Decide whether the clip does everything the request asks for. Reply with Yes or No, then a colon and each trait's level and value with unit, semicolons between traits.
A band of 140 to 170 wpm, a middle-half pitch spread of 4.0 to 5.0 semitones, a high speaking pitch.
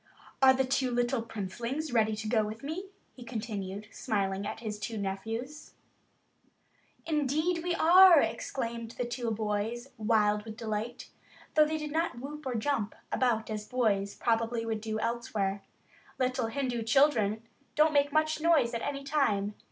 Yes: average, 160 wpm; average, 4.4 semitones; high, 235 Hz